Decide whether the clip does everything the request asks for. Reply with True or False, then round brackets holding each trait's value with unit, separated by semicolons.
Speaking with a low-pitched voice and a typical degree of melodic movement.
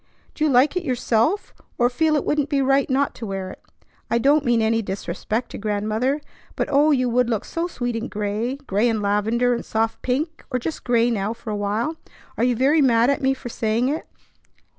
False (245 Hz; 3.9 semitones)